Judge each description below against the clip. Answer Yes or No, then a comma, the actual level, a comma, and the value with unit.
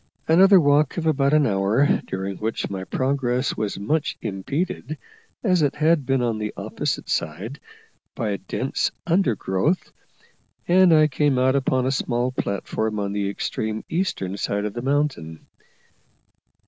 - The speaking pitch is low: Yes, low, 130 Hz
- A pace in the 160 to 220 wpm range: No, average, 150 wpm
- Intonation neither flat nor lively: No, wide, 6.5 semitones